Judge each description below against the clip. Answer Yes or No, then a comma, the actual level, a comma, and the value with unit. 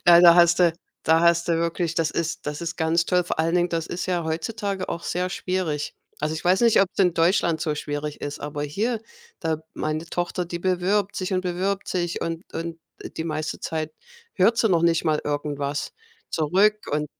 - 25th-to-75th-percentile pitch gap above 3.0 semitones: No, narrow, 2.4 semitones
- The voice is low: No, medium, 170 Hz